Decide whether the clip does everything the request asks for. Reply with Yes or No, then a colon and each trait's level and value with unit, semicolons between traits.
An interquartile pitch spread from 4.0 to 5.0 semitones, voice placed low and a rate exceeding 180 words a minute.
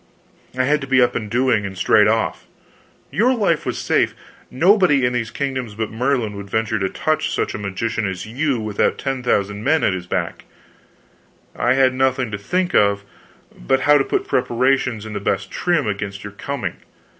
Yes: average, 4.7 semitones; low, 120 Hz; average, 190 wpm